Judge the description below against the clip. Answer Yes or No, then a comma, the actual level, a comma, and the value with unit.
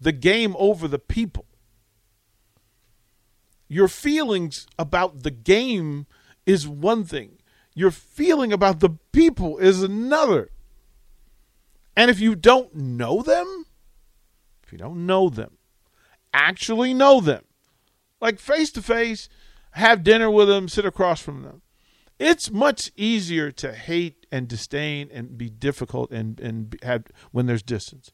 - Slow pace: Yes, slow, 130 wpm